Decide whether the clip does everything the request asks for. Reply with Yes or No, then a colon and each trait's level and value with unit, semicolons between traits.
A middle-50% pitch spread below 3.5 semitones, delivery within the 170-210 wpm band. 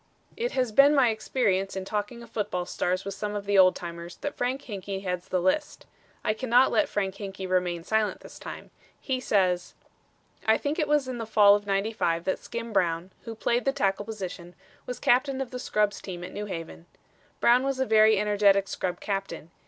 No: average, 4.3 semitones; average, 200 wpm